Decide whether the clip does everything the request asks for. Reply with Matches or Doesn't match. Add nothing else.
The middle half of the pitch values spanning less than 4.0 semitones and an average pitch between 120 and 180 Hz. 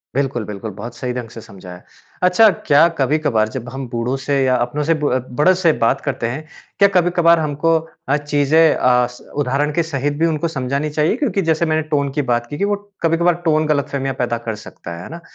Doesn't match